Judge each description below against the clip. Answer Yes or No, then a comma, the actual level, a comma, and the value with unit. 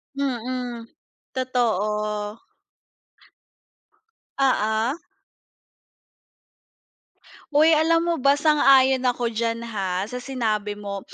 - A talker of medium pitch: No, high, 240 Hz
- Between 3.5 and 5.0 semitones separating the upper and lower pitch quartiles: Yes, average, 4.0 semitones